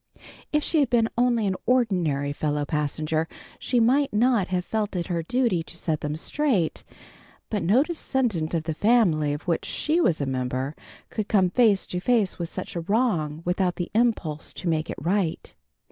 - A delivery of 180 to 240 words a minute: Yes, average, 185 wpm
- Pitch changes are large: Yes, wide, 6.7 semitones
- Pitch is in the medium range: Yes, medium, 180 Hz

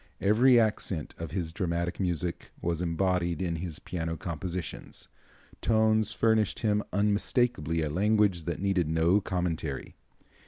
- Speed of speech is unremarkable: No, slow, 125 wpm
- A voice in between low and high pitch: No, very low, 90 Hz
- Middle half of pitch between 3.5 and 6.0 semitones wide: Yes, average, 4.0 semitones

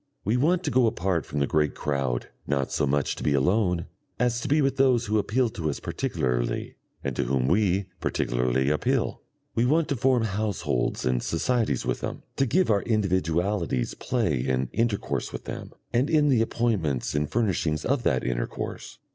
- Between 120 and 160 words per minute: No, average, 180 wpm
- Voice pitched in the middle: No, low, 100 Hz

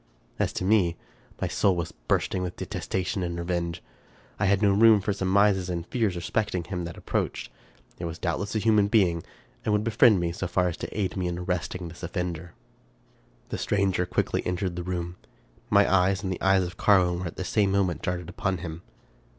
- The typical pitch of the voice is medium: No, very low, 90 Hz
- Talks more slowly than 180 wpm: No, average, 200 wpm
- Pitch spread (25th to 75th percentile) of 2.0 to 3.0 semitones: Yes, narrow, 2.4 semitones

